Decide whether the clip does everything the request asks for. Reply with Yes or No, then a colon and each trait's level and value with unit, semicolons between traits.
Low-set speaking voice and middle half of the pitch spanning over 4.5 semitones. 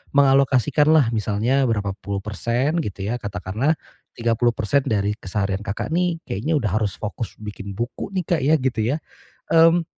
Yes: low, 115 Hz; wide, 5.5 semitones